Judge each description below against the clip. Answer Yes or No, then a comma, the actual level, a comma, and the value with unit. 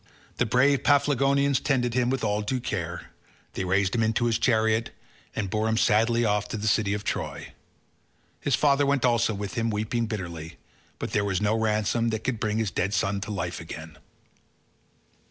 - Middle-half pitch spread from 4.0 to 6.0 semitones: No, average, 2.9 semitones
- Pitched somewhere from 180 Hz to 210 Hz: No, low, 110 Hz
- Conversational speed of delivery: Yes, average, 185 wpm